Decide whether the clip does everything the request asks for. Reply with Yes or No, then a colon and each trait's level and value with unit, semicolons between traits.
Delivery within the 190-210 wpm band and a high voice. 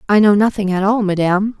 No: fast, 225 wpm; high, 200 Hz